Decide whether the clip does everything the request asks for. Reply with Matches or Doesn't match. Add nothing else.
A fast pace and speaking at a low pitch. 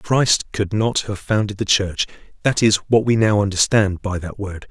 Matches